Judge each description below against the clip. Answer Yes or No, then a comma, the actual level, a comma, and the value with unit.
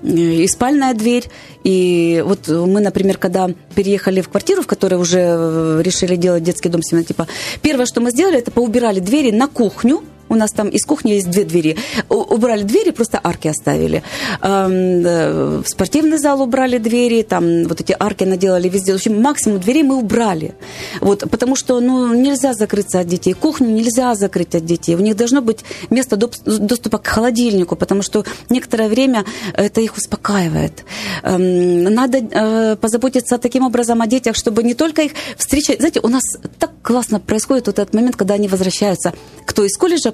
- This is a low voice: No, high, 215 Hz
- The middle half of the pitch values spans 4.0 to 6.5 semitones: Yes, average, 4.9 semitones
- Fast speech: Yes, fast, 165 wpm